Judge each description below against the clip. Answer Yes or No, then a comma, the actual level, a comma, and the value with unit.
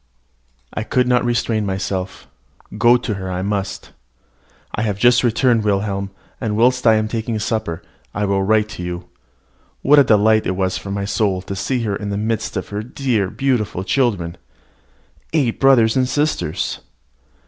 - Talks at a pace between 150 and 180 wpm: Yes, average, 170 wpm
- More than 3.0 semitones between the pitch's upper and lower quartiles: Yes, average, 3.5 semitones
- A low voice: Yes, low, 110 Hz